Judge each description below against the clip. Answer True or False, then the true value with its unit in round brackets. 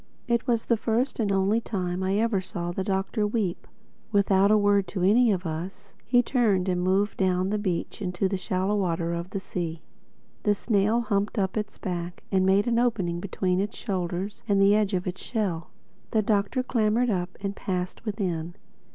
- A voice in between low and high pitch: False (195 Hz)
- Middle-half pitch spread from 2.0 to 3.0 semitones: True (2.7 semitones)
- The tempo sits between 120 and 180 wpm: False (190 wpm)